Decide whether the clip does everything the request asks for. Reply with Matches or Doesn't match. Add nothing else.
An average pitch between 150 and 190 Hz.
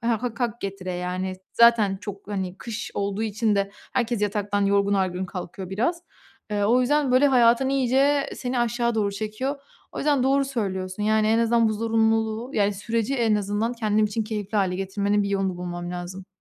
Doesn't match